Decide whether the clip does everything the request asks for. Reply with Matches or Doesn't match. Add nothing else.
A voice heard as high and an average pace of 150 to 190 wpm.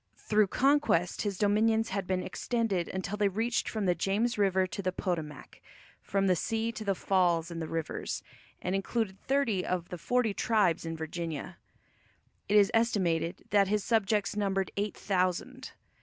Matches